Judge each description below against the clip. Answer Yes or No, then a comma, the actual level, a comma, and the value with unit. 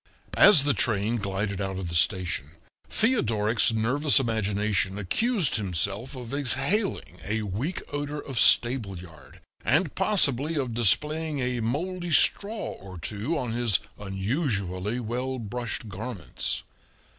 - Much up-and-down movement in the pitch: Yes, wide, 6.3 semitones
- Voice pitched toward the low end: Yes, low, 115 Hz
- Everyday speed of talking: No, slow, 125 wpm